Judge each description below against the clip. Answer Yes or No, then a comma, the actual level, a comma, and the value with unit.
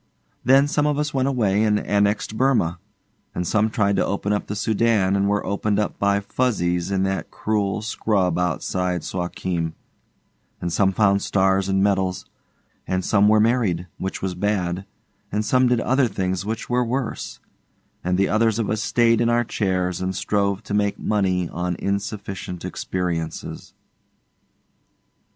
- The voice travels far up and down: No, average, 2.9 semitones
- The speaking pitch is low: Yes, low, 100 Hz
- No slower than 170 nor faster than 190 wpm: No, average, 160 wpm